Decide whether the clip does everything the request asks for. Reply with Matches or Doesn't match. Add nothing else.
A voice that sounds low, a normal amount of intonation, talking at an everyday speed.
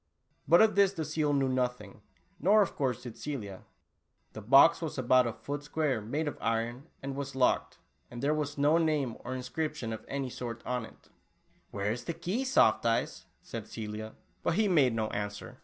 Matches